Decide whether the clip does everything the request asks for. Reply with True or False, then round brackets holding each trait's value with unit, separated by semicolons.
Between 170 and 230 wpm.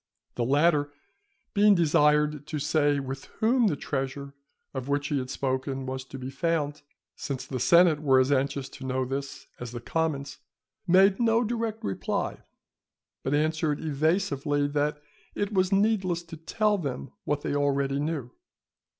False (155 wpm)